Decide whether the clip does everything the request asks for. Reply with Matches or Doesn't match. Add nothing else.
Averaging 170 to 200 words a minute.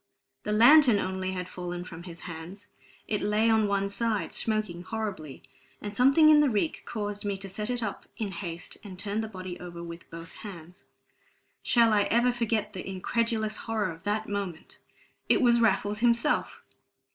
Matches